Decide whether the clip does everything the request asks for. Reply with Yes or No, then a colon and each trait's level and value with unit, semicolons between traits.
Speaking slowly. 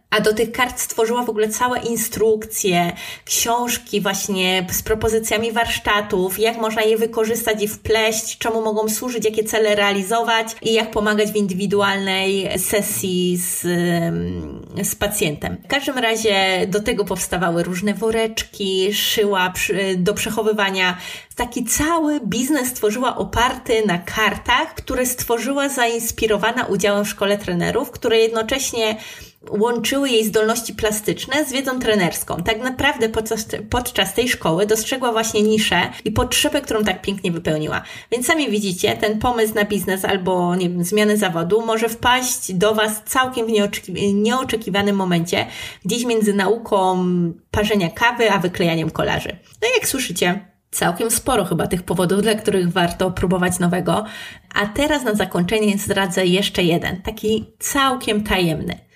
No: average, 140 wpm